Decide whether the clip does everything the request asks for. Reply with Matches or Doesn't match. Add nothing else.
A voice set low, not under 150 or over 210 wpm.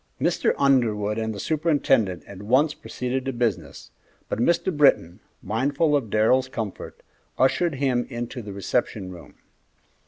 Doesn't match